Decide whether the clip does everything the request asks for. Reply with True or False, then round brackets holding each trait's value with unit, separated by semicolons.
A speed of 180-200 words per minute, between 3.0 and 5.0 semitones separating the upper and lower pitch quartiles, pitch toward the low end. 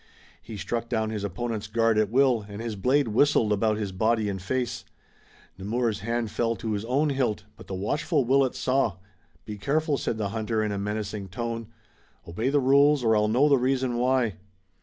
True (190 wpm; 3.4 semitones; 115 Hz)